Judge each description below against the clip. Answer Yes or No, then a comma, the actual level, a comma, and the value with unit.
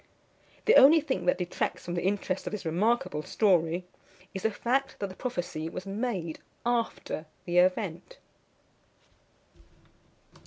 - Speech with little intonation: No, average, 5.3 semitones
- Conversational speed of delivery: No, slow, 130 wpm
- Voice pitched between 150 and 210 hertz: Yes, high, 190 Hz